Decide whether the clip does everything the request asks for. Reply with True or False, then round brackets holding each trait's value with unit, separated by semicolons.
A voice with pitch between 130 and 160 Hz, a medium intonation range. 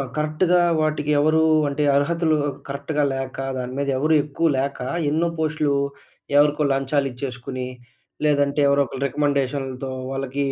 False (140 Hz; 2.0 semitones)